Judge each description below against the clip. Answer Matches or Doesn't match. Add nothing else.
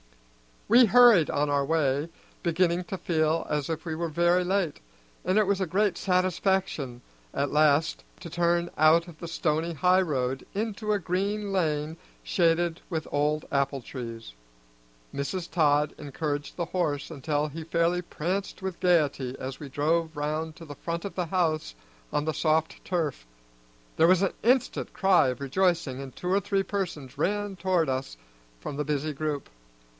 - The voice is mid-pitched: Matches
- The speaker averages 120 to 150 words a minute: Doesn't match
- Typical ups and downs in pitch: Matches